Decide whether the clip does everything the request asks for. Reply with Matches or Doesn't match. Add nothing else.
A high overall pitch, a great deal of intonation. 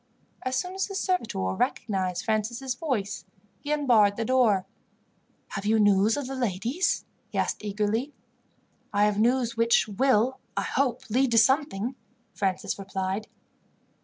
Doesn't match